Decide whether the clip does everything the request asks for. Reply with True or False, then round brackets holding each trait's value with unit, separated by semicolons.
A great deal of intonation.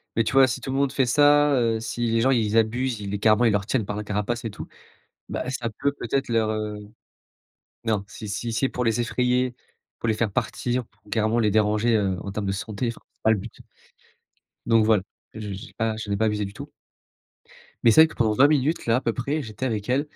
False (2.9 semitones)